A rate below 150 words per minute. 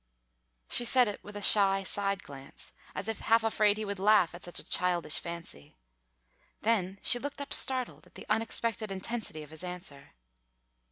No: average, 175 wpm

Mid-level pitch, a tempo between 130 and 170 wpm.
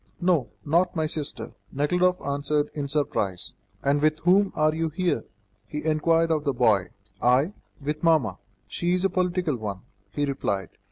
Yes: medium, 150 Hz; average, 160 wpm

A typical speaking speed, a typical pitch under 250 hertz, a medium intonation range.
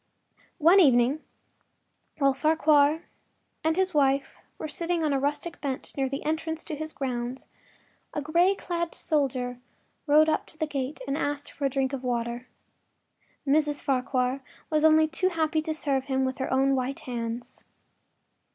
No: average, 160 wpm; very high, 285 Hz; average, 3.0 semitones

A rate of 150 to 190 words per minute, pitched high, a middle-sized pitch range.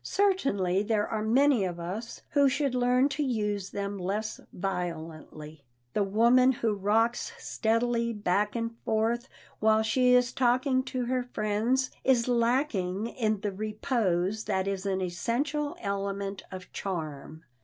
No: average, 140 wpm; high, 220 Hz; average, 4.2 semitones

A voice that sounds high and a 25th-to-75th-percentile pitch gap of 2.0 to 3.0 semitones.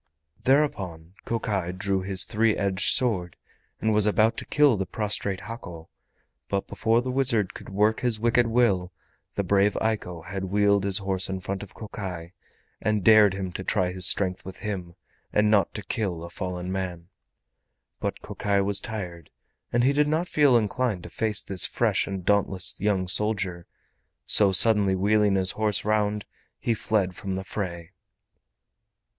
No: low, 100 Hz; average, 2.7 semitones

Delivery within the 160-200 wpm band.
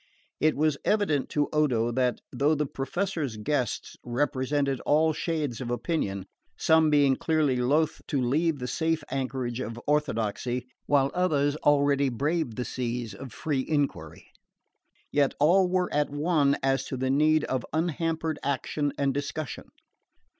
No: average, 145 wpm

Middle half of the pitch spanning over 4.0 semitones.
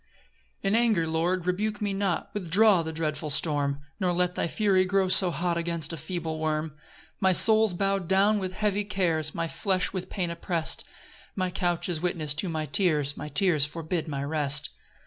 No: average, 3.4 semitones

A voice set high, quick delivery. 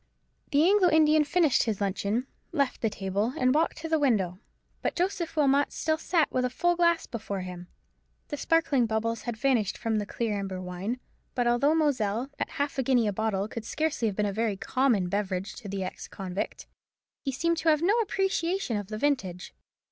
No: high, 245 Hz; average, 195 wpm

